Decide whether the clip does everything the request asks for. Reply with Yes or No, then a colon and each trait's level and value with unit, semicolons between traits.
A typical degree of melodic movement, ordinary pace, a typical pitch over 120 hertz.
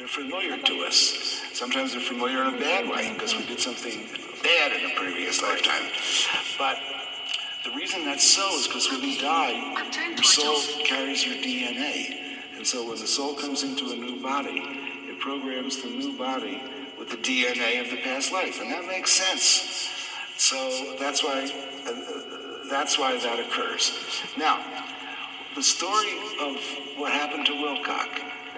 No: narrow, 1.8 semitones; average, 160 wpm; medium, 140 Hz